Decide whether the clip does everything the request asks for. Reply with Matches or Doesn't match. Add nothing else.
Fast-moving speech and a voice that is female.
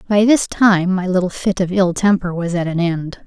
Matches